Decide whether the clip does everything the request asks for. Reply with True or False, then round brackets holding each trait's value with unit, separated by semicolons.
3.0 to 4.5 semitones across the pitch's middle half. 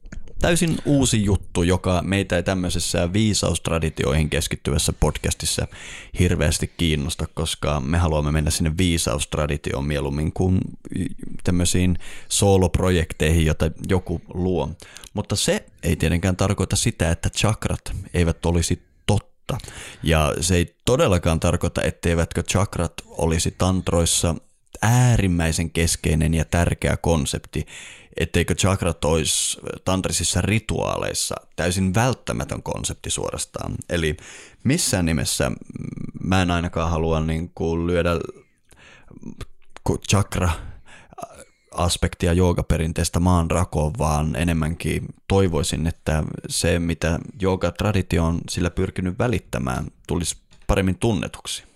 False (2.5 semitones)